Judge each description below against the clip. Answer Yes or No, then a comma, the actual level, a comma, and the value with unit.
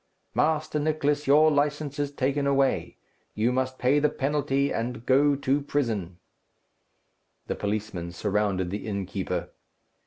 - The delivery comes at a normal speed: No, slow, 125 wpm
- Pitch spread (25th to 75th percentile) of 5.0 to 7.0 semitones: Yes, wide, 5.5 semitones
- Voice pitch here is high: No, low, 135 Hz